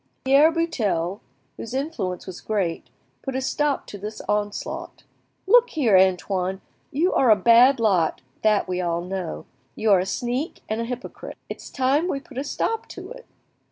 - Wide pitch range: Yes, wide, 6.6 semitones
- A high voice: Yes, high, 225 Hz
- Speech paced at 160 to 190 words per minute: Yes, average, 170 wpm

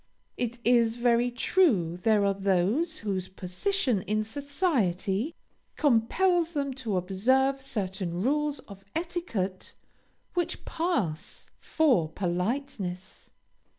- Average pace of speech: No, slow, 100 wpm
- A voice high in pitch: Yes, high, 230 Hz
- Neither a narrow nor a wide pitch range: No, wide, 7.1 semitones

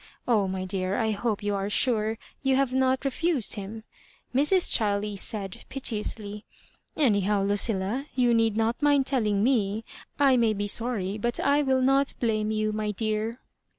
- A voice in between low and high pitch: No, high, 220 Hz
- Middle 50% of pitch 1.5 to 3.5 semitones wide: No, average, 4.0 semitones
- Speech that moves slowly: No, average, 165 wpm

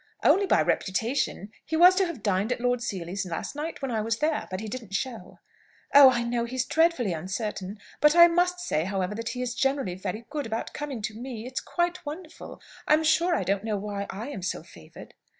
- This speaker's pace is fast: Yes, fast, 215 wpm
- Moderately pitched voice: No, high, 235 Hz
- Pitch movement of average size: No, wide, 6.8 semitones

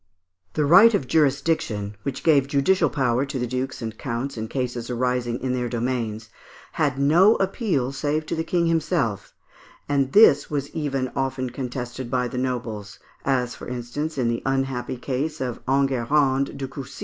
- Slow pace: No, average, 165 wpm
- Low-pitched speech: Yes, low, 130 Hz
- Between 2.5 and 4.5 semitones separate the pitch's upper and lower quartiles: Yes, average, 2.8 semitones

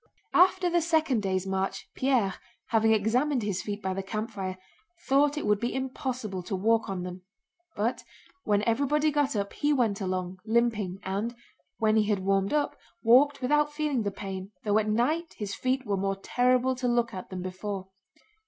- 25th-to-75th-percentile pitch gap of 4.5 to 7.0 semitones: Yes, average, 5.0 semitones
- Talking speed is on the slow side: No, average, 180 wpm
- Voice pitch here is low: No, high, 220 Hz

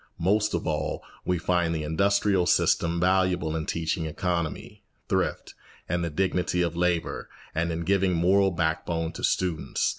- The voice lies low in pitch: Yes, very low, 85 Hz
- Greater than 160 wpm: No, average, 150 wpm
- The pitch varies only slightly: Yes, narrow, 2.0 semitones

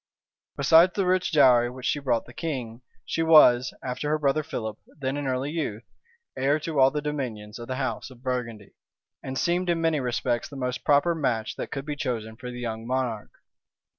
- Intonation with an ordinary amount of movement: Yes, average, 3.6 semitones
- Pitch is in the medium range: No, low, 130 Hz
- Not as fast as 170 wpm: No, average, 195 wpm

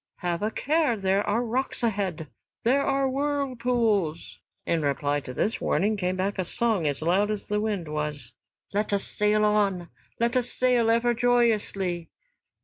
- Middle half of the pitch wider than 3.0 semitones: Yes, average, 5.1 semitones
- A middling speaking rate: Yes, average, 160 wpm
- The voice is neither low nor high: No, high, 210 Hz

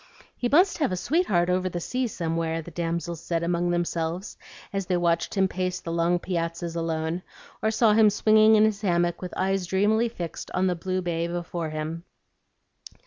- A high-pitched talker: No, medium, 175 Hz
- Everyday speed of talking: Yes, average, 185 wpm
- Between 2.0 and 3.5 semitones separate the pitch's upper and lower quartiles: Yes, average, 2.8 semitones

